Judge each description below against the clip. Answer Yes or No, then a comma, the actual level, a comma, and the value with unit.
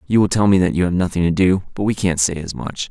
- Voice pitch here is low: Yes, very low, 90 Hz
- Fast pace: Yes, fast, 330 wpm